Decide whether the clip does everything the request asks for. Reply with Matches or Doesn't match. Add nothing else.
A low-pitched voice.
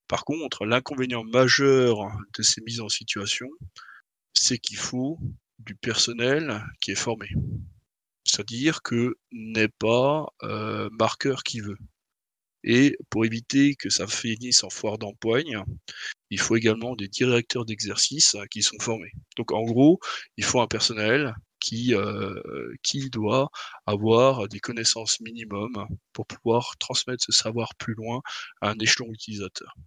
Matches